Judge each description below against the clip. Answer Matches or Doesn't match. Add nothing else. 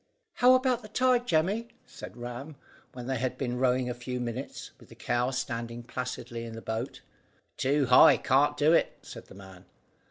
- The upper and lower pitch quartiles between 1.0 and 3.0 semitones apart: Doesn't match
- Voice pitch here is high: Doesn't match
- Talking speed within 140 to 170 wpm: Doesn't match